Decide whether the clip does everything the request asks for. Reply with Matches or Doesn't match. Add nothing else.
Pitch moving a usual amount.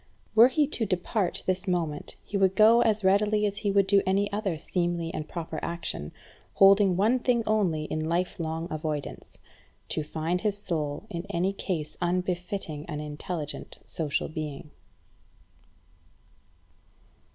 Matches